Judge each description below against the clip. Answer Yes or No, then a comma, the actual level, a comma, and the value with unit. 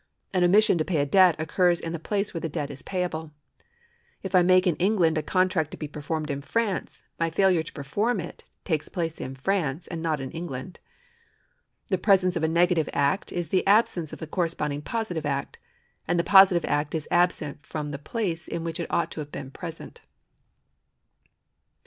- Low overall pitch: No, medium, 165 Hz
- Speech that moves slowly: No, average, 195 wpm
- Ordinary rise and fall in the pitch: Yes, average, 3.3 semitones